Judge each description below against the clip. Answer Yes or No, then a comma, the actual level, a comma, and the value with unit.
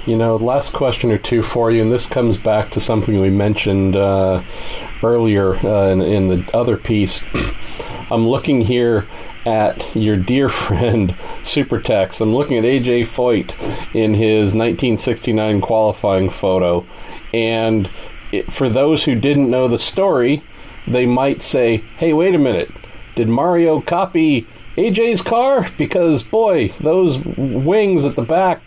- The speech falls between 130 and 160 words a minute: Yes, average, 145 wpm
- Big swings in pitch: No, average, 4.0 semitones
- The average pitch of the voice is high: No, low, 115 Hz